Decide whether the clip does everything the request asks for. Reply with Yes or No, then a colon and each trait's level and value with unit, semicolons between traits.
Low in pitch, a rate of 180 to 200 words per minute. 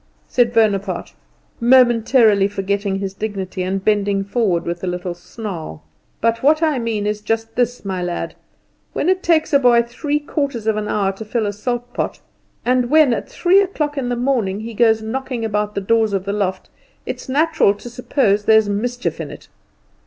No: high, 220 Hz; average, 185 wpm